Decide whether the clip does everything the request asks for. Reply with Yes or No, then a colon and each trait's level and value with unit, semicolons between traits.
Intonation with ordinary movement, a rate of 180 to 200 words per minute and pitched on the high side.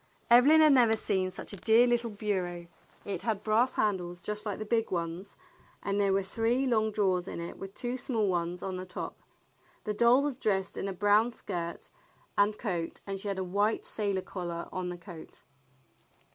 Yes: average, 3.6 semitones; average, 195 wpm; high, 205 Hz